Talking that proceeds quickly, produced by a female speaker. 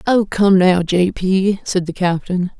No: average, 185 wpm; female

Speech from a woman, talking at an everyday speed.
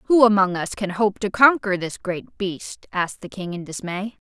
No: female; fast, 210 wpm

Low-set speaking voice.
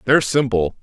Yes: low, 120 Hz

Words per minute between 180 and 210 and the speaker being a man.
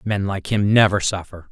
Yes: average, 200 wpm; male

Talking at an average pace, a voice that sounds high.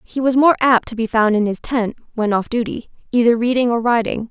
No: fast, 235 wpm; high, 235 Hz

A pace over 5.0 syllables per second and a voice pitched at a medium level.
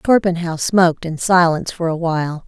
Yes: 5.4 syllables/s; medium, 170 Hz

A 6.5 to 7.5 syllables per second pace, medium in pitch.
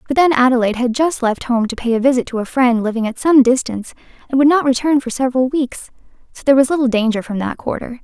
No: 6.6 syllables/s; very high, 255 Hz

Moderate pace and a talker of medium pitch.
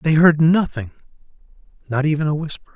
Yes: average, 150 wpm; medium, 150 Hz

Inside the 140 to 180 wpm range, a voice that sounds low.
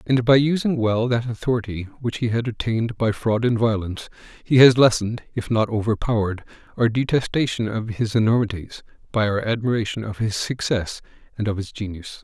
Yes: average, 170 wpm; low, 115 Hz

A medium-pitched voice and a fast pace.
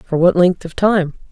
Yes: medium, 175 Hz; fast, 230 wpm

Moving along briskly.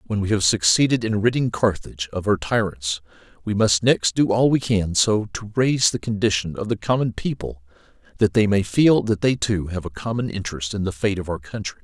Yes: fast, 220 wpm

